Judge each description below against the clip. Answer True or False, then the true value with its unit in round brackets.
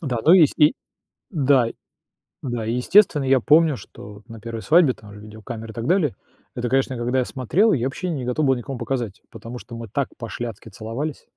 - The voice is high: False (125 Hz)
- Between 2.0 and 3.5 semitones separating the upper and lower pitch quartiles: False (4.1 semitones)